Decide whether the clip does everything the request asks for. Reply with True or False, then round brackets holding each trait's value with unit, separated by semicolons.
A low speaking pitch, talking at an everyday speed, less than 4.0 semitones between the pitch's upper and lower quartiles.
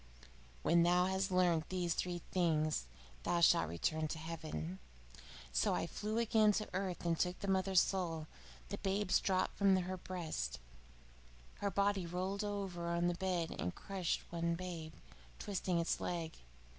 False (180 Hz; 150 wpm; 2.4 semitones)